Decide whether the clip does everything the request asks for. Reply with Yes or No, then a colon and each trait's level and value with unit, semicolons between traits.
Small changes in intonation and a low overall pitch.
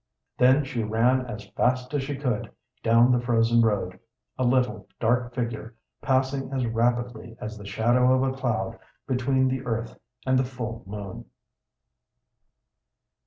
Yes: narrow, 2.3 semitones; low, 120 Hz